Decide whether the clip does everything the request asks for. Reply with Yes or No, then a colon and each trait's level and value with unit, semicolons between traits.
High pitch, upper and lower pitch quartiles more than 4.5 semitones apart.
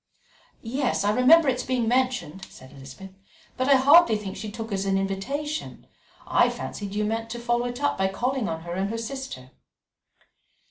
Yes: high, 225 Hz; average, 5.0 semitones